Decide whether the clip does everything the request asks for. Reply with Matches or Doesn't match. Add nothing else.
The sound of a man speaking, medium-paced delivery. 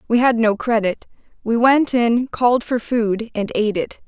Doesn't match